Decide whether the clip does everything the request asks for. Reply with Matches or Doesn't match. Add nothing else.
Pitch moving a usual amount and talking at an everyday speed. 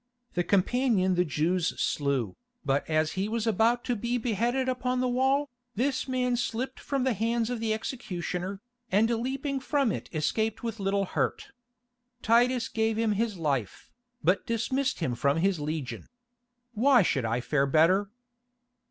Doesn't match